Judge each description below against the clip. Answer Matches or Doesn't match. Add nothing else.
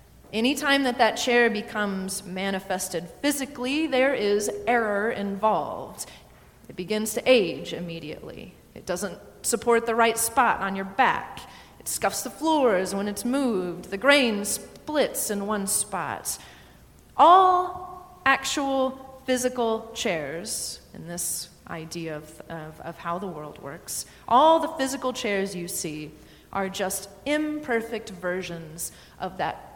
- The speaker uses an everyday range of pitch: Doesn't match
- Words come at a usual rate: Doesn't match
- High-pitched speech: Matches